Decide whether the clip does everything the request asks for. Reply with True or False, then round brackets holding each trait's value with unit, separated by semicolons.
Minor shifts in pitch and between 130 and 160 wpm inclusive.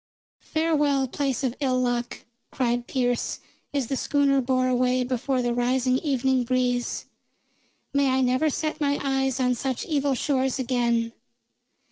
True (1.9 semitones; 140 wpm)